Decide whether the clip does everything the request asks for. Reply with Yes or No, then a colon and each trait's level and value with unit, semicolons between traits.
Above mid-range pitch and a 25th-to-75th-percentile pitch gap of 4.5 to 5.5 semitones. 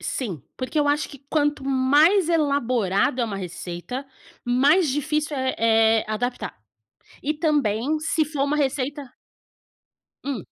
No: very high, 275 Hz; average, 3.8 semitones